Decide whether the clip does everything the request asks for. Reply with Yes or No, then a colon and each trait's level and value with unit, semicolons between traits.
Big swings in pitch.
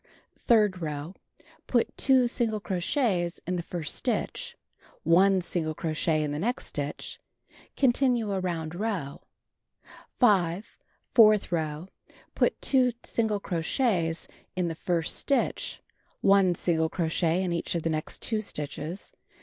No: average, 4.7 semitones